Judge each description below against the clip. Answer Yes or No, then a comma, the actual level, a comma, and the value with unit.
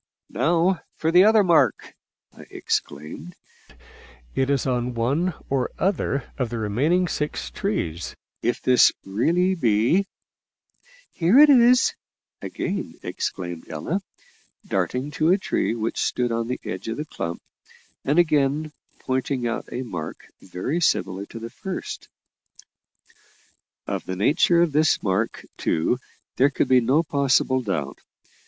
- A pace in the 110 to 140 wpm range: Yes, slow, 135 wpm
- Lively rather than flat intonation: Yes, wide, 6.9 semitones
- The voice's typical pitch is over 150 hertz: No, low, 135 Hz